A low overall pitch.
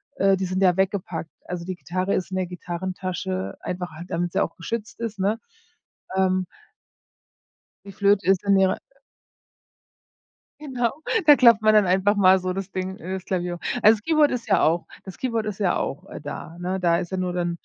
No: medium, 185 Hz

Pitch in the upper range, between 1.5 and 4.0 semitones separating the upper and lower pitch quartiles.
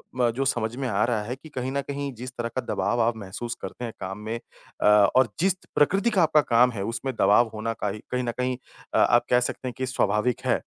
No: low, 120 Hz; average, 2.8 semitones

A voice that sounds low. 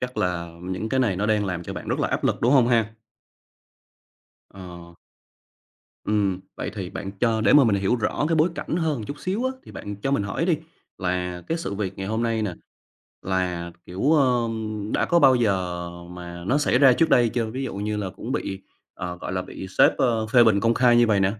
Yes: low, 110 Hz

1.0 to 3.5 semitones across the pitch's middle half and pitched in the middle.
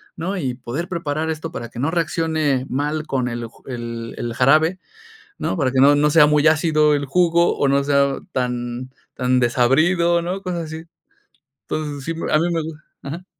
No: average, 4.1 semitones; medium, 150 Hz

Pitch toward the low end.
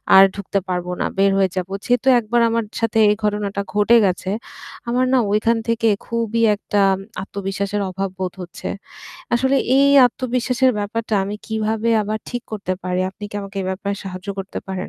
No: high, 210 Hz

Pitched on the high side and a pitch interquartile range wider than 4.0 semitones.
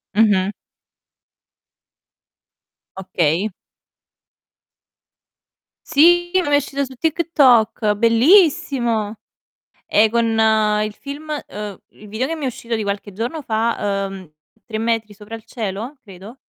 Yes: high, 225 Hz; average, 5.2 semitones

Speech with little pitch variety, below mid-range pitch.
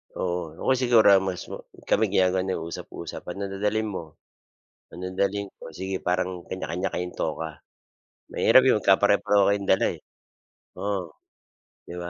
Yes: narrow, 2.0 semitones; very low, 95 Hz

